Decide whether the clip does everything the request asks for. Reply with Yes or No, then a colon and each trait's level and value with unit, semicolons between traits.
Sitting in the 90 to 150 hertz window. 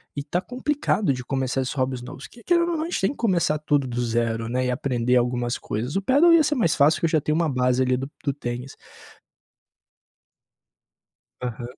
Yes: low, 135 Hz